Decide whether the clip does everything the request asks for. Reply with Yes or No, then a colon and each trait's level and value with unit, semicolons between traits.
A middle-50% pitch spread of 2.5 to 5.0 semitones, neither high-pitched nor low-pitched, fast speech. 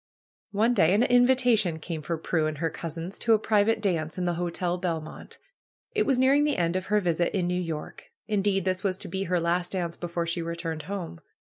Yes: average, 3.6 semitones; medium, 180 Hz; fast, 215 wpm